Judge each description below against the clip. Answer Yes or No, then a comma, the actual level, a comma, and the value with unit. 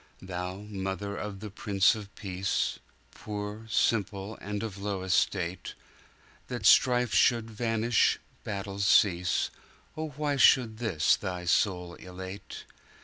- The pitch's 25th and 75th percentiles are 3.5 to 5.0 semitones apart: No, average, 2.7 semitones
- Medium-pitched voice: No, low, 100 Hz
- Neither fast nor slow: No, slow, 105 wpm